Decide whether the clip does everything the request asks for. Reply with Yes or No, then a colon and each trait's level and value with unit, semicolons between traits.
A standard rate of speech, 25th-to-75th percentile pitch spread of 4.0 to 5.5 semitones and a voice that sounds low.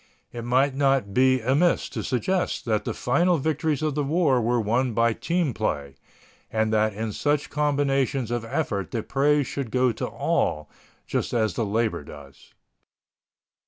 Yes: average, 160 wpm; average, 4.6 semitones; low, 130 Hz